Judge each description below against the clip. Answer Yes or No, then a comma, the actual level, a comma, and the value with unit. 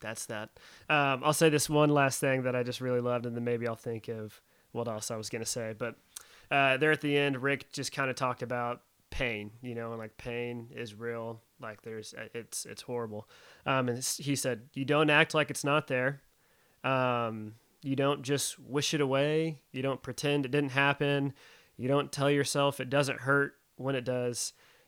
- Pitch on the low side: Yes, low, 130 Hz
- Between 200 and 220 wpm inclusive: Yes, fast, 205 wpm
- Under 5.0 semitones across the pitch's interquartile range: Yes, average, 3.0 semitones